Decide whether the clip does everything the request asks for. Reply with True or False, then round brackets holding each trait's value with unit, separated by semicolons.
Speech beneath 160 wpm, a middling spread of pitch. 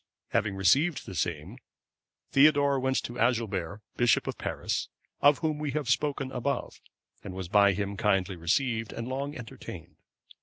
False (150 wpm; 5.9 semitones)